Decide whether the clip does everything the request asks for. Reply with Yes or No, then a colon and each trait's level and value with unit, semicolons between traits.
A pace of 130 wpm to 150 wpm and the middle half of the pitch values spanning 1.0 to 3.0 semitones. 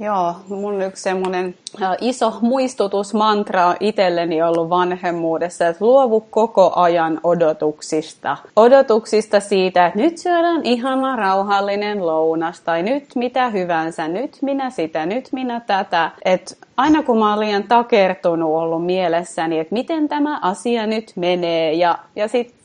No: average, 135 wpm; wide, 5.6 semitones